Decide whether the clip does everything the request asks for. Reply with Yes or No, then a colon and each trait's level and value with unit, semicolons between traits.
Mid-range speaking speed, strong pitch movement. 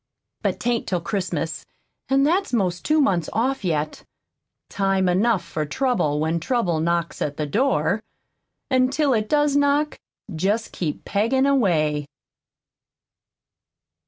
No: slow, 130 wpm; wide, 8.0 semitones